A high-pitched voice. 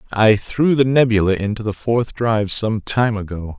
No: low, 110 Hz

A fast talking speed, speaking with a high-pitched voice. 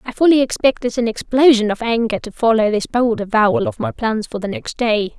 Yes: fast, 220 wpm; high, 225 Hz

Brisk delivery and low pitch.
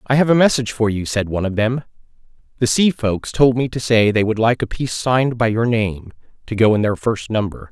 Yes: fast, 250 wpm; low, 115 Hz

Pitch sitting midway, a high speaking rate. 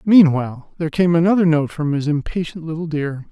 No: medium, 160 Hz; average, 180 wpm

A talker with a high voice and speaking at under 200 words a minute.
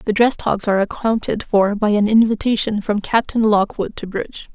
Yes: high, 210 Hz; average, 185 wpm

